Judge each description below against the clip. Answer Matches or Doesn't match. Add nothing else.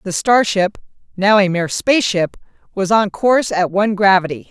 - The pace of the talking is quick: Doesn't match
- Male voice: Doesn't match